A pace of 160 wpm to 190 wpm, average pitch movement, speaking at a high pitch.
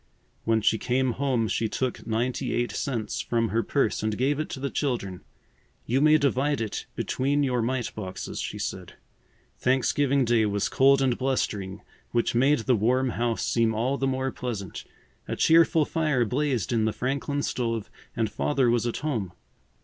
No: average, 170 wpm; average, 3.3 semitones; low, 125 Hz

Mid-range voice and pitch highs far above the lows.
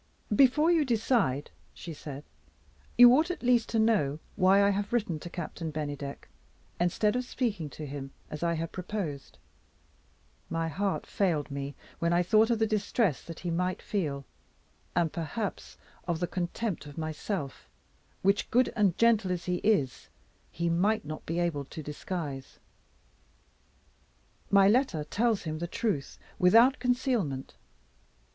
Yes: medium, 180 Hz; wide, 6.0 semitones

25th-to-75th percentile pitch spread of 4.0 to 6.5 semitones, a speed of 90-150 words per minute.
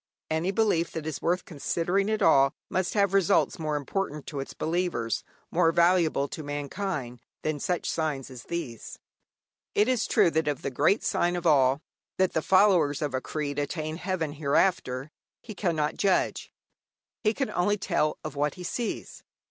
No: average, 4.3 semitones; average, 170 wpm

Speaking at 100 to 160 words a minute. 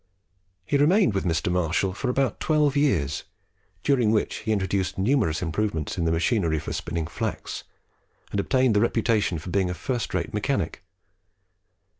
Yes: average, 155 wpm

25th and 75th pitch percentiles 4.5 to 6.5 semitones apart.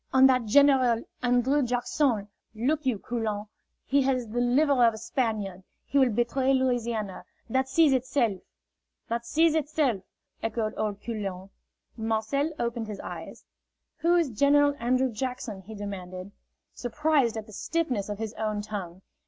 No: average, 3.8 semitones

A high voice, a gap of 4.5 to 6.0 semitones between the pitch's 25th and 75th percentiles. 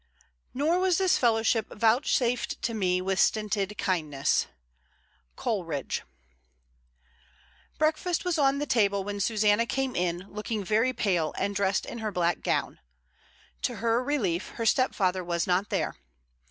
Yes: high, 210 Hz; average, 5.0 semitones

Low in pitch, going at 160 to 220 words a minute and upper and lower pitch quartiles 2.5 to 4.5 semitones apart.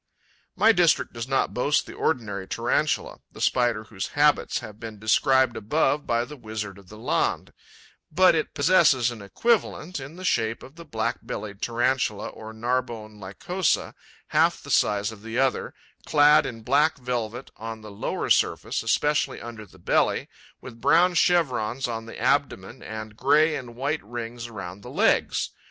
No: low, 120 Hz; average, 165 wpm; average, 5.0 semitones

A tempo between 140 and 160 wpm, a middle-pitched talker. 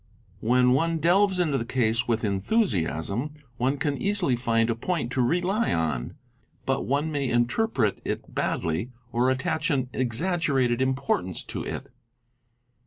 No: average, 150 wpm; low, 130 Hz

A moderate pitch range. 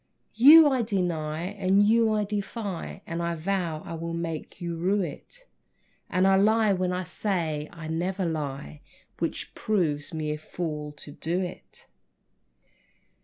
Yes: average, 4.1 semitones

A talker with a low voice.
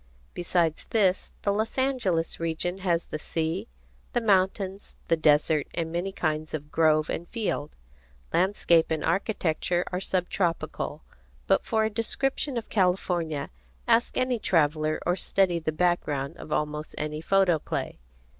No: medium, 175 Hz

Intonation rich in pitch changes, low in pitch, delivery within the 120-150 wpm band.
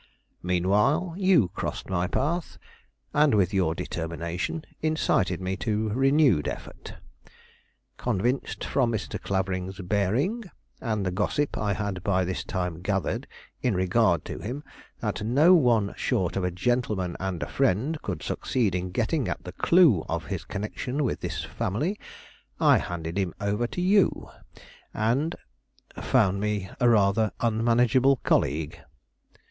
Yes: wide, 5.9 semitones; low, 105 Hz; average, 140 wpm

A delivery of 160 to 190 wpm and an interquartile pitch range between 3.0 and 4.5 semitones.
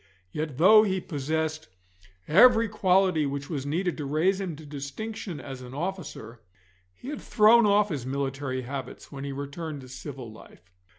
No: average, 165 wpm; wide, 5.6 semitones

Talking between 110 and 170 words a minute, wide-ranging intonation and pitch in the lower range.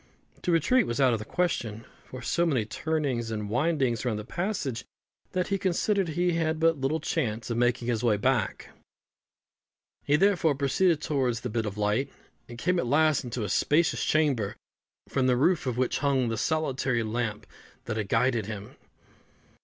No: average, 180 wpm; wide, 5.7 semitones; low, 130 Hz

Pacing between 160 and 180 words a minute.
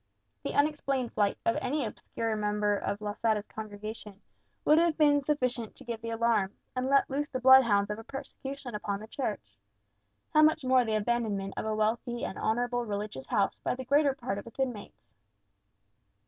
Yes: average, 175 wpm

